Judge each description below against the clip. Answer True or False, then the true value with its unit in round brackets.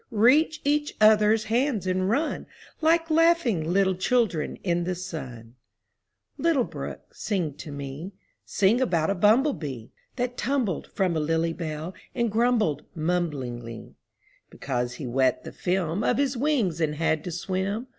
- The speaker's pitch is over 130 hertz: True (185 Hz)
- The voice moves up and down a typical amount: False (7.5 semitones)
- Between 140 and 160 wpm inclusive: True (145 wpm)